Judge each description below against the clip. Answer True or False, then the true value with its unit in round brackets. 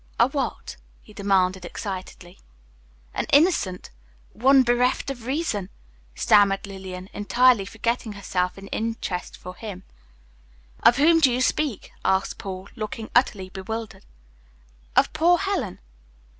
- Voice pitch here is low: False (210 Hz)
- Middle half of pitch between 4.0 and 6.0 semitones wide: True (4.9 semitones)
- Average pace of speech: False (125 wpm)